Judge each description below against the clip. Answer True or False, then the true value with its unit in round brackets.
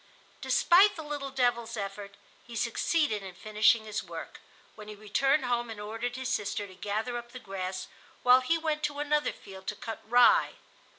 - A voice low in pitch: False (235 Hz)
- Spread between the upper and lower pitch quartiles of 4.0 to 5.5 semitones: True (4.5 semitones)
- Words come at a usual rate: True (180 wpm)